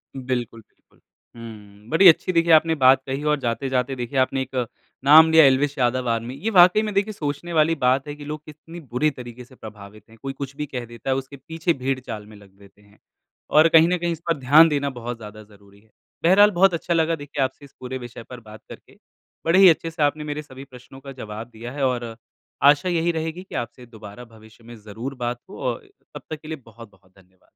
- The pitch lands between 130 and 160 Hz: Yes, low, 135 Hz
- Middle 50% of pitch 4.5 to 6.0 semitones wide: Yes, average, 5.1 semitones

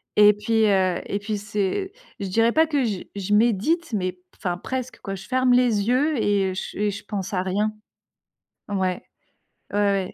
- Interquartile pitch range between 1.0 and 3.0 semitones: No, average, 3.5 semitones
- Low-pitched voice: No, high, 205 Hz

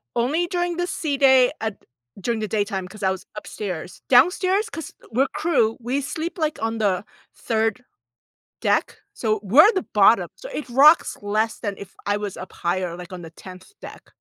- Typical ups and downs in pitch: No, wide, 7.2 semitones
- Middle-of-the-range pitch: No, high, 225 Hz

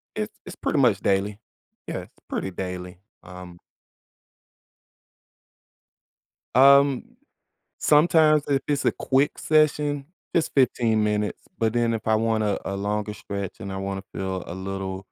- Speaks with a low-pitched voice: Yes, low, 105 Hz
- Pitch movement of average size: No, wide, 6.1 semitones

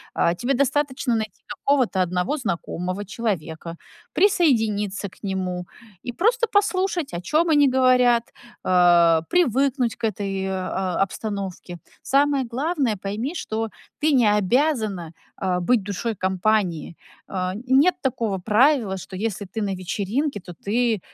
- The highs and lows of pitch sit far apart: Yes, wide, 6.3 semitones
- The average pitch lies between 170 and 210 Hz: No, high, 220 Hz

